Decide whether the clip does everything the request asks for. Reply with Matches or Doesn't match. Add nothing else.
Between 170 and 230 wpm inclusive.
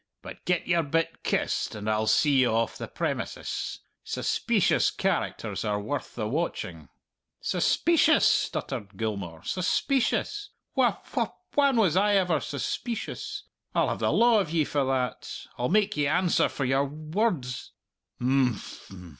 Doesn't match